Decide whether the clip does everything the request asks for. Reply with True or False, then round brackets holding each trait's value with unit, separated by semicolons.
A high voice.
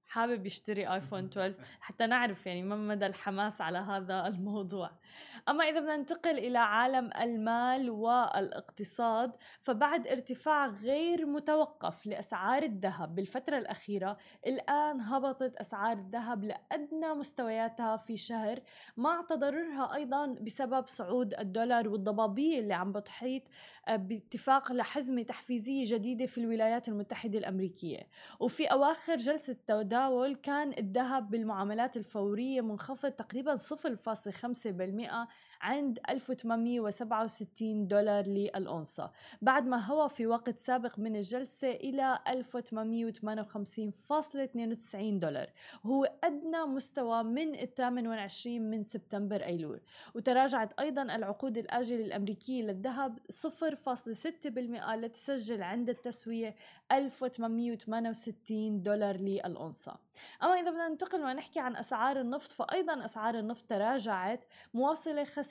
True (235 Hz)